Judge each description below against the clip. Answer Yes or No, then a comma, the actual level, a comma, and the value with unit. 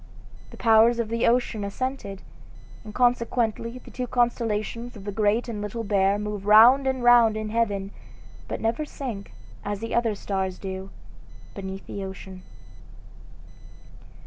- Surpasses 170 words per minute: No, average, 145 wpm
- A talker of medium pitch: No, high, 220 Hz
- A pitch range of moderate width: Yes, average, 3.0 semitones